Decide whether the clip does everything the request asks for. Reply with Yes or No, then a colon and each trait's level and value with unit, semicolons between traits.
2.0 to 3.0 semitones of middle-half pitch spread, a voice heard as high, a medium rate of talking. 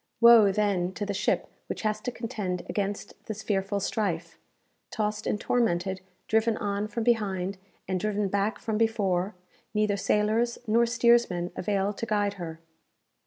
Yes: narrow, 2.4 semitones; high, 210 Hz; average, 150 wpm